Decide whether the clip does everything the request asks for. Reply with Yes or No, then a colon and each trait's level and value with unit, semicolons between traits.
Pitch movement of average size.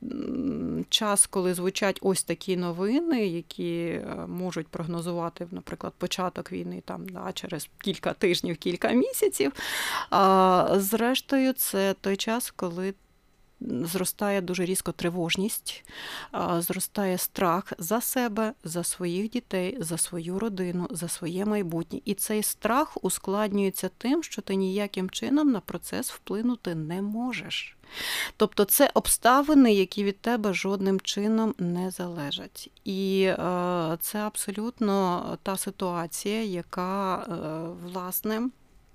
Yes: average, 3.4 semitones